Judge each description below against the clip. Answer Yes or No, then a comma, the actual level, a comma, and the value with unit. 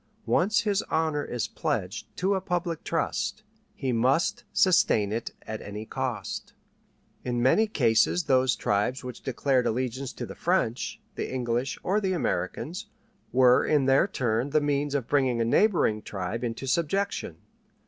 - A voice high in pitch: No, low, 130 Hz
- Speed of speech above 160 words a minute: No, average, 150 wpm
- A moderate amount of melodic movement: No, wide, 5.9 semitones